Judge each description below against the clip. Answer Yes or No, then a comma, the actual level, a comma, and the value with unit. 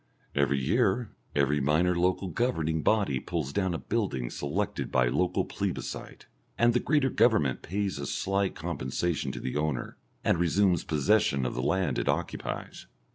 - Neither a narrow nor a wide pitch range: No, wide, 5.8 semitones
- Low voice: Yes, very low, 85 Hz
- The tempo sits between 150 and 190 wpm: Yes, average, 155 wpm